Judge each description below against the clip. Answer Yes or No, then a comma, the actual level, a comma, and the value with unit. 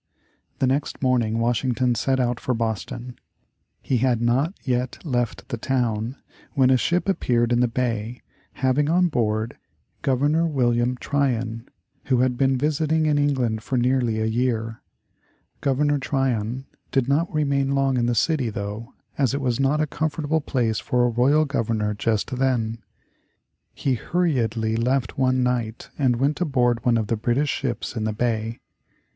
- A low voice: Yes, low, 125 Hz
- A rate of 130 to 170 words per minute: Yes, average, 160 wpm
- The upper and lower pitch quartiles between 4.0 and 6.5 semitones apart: No, average, 3.0 semitones